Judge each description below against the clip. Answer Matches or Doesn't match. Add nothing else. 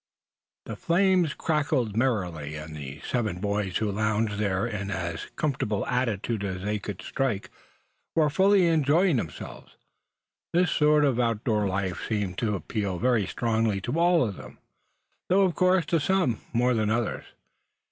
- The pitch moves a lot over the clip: Matches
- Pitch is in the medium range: Doesn't match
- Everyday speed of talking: Matches